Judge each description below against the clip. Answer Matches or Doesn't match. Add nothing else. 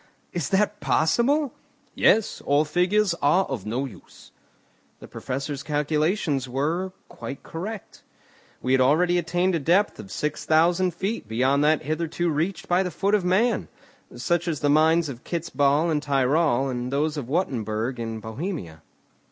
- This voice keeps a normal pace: Matches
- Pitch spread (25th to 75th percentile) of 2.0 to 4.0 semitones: Doesn't match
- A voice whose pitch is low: Doesn't match